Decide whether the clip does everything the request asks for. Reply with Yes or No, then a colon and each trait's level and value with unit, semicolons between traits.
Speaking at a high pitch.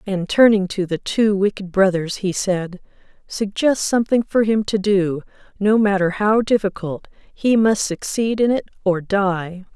Yes: high, 200 Hz